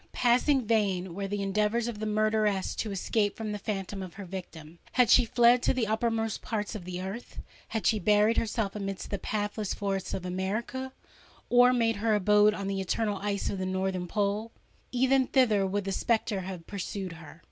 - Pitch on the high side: Yes, high, 210 Hz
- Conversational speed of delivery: Yes, average, 180 wpm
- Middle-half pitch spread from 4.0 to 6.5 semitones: No, average, 2.7 semitones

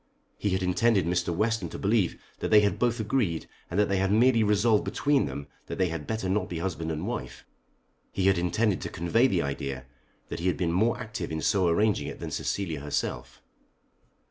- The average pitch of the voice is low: Yes, very low, 95 Hz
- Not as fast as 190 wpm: No, fast, 205 wpm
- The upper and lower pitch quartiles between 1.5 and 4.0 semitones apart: No, average, 4.4 semitones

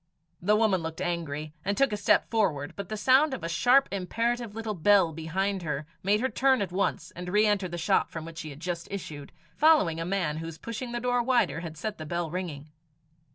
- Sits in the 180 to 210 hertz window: Yes, medium, 185 Hz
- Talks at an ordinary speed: No, fast, 220 wpm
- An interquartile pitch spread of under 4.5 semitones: No, average, 5.0 semitones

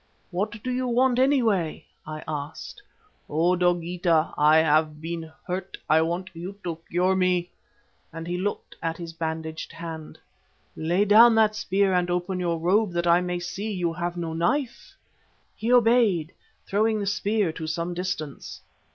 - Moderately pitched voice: Yes, medium, 175 Hz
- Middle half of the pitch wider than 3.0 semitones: Yes, average, 3.8 semitones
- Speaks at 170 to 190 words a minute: No, average, 160 wpm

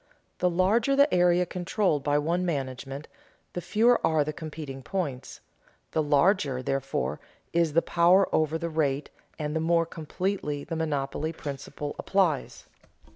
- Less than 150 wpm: Yes, average, 140 wpm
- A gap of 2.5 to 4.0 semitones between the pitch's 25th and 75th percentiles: Yes, average, 3.6 semitones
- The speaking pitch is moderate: Yes, medium, 160 Hz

